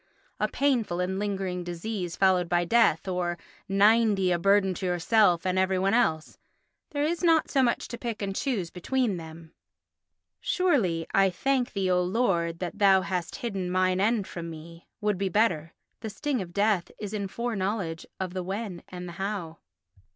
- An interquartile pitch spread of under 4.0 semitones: Yes, average, 3.6 semitones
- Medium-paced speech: Yes, average, 175 wpm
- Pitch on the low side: No, high, 190 Hz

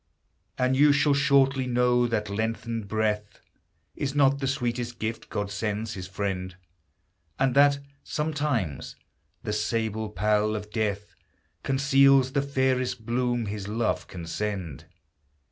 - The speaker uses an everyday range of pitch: Yes, average, 4.2 semitones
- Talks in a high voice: No, low, 115 Hz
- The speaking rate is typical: No, slow, 130 wpm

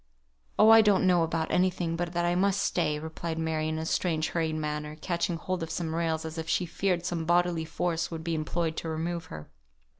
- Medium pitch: Yes, medium, 165 Hz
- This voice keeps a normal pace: No, fast, 220 wpm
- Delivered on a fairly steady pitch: Yes, narrow, 1.7 semitones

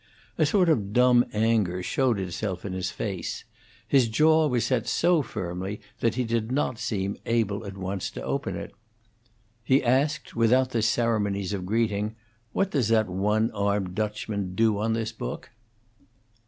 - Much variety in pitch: No, average, 3.4 semitones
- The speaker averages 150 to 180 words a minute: Yes, average, 160 wpm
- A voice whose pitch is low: Yes, low, 110 Hz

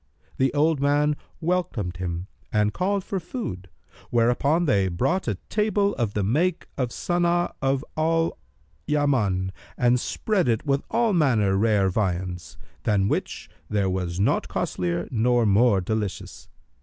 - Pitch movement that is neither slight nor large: No, wide, 8.7 semitones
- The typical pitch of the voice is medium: No, low, 120 Hz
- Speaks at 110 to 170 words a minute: Yes, average, 140 wpm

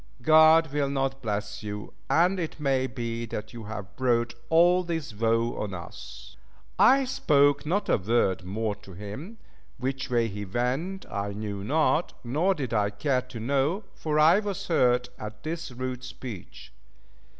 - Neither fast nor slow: Yes, average, 160 wpm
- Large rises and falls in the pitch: Yes, wide, 6.6 semitones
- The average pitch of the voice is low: Yes, low, 125 Hz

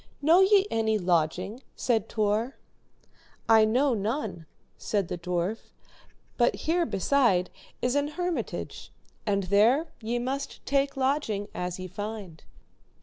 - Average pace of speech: No, slow, 125 wpm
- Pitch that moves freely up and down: Yes, wide, 5.9 semitones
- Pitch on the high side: Yes, high, 225 Hz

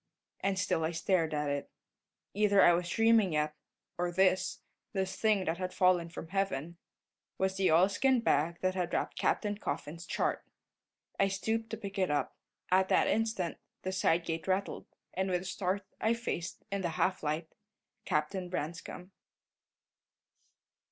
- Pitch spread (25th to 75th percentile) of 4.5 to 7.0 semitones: No, average, 2.8 semitones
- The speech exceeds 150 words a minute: Yes, average, 160 wpm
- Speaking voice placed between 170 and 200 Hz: Yes, medium, 185 Hz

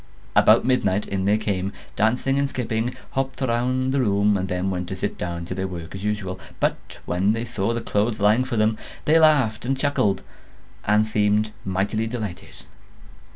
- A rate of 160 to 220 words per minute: Yes, average, 180 wpm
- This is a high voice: No, low, 105 Hz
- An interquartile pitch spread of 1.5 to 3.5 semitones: No, average, 4.0 semitones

